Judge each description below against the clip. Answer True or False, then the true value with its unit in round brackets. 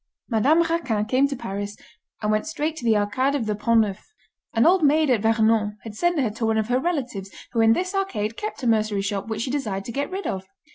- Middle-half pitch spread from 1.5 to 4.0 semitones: False (5.1 semitones)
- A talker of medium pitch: False (230 Hz)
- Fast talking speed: True (240 wpm)